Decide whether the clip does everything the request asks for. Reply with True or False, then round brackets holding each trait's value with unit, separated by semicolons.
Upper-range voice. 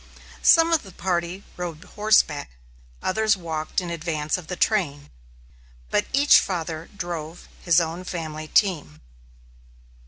False (170 Hz)